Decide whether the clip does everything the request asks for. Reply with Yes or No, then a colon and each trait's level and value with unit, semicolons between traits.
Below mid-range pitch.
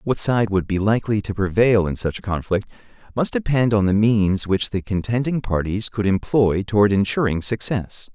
Yes: low, 105 Hz